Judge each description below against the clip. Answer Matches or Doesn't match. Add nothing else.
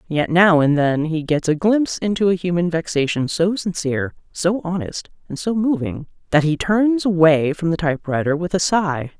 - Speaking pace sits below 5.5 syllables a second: Matches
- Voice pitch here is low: Doesn't match